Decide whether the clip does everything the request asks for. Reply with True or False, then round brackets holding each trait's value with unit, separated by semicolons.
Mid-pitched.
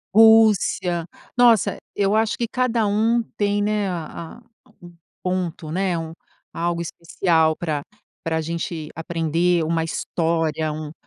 True (175 Hz)